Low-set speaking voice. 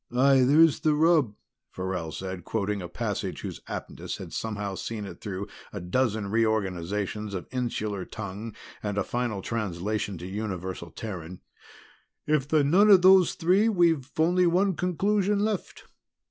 Yes: low, 110 Hz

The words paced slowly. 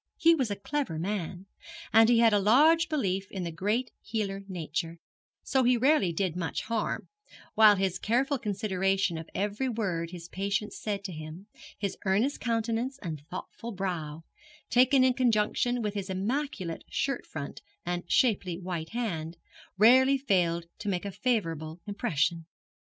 No: average, 155 wpm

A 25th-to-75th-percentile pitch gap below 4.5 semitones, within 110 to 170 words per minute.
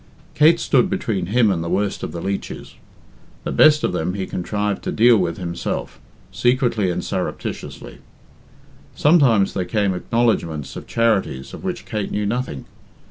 No: average, 5.1 semitones; average, 155 wpm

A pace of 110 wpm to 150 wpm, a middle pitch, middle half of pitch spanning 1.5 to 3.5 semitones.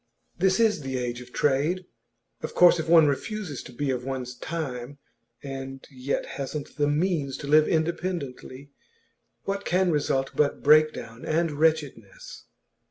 No: average, 145 wpm; medium, 145 Hz; average, 4.0 semitones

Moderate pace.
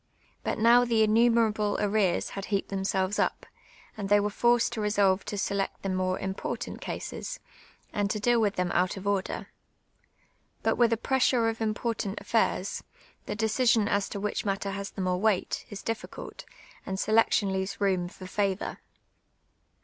Yes: average, 165 wpm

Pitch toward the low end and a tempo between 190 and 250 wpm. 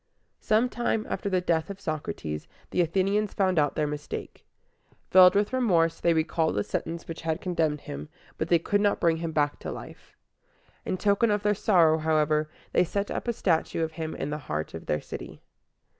No: medium, 165 Hz; average, 195 wpm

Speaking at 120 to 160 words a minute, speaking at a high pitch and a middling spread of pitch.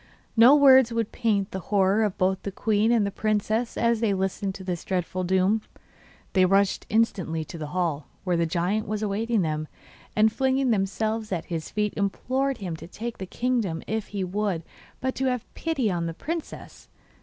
No: average, 190 wpm; high, 205 Hz; average, 3.7 semitones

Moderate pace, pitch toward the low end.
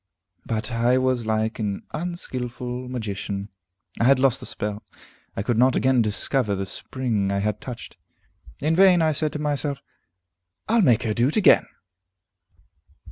Yes: average, 155 wpm; low, 125 Hz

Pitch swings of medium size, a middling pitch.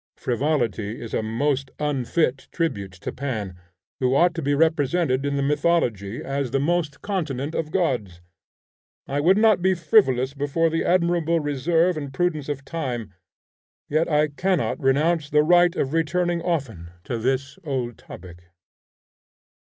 Yes: average, 4.5 semitones; medium, 145 Hz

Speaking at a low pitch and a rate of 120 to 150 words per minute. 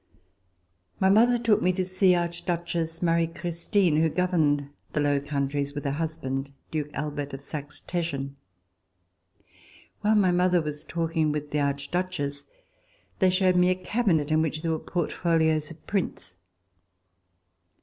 No: medium, 165 Hz; average, 140 wpm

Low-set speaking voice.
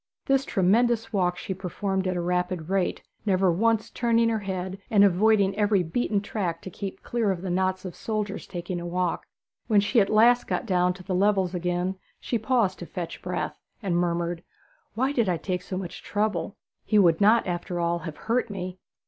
No: high, 190 Hz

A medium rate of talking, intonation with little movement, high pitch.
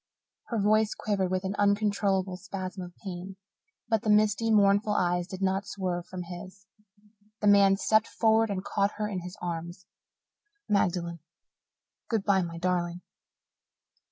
Yes: average, 145 wpm; narrow, 2.3 semitones; high, 195 Hz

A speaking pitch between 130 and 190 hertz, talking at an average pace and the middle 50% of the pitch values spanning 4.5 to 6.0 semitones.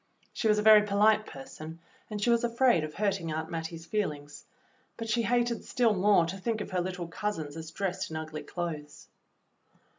Yes: medium, 185 Hz; average, 185 wpm; average, 5.1 semitones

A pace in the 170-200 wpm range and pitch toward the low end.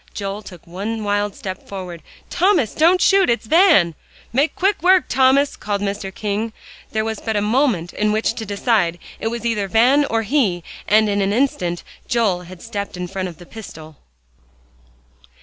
No: average, 175 wpm; high, 215 Hz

